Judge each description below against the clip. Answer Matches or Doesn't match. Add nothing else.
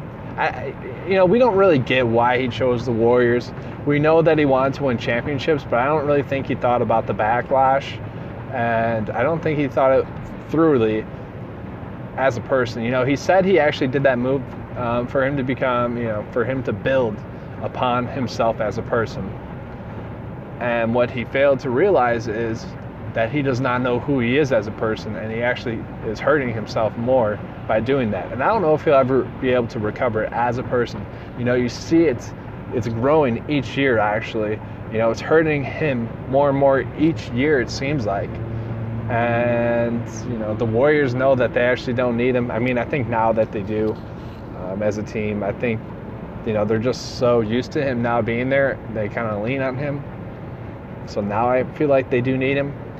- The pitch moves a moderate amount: Matches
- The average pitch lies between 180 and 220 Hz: Doesn't match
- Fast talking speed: Matches